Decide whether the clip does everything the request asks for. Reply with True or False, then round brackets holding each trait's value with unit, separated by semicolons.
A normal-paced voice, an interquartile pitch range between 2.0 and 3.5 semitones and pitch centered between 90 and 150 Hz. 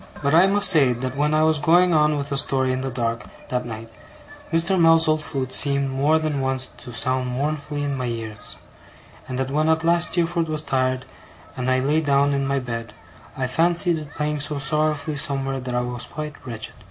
False (210 wpm; 3.2 semitones; 140 Hz)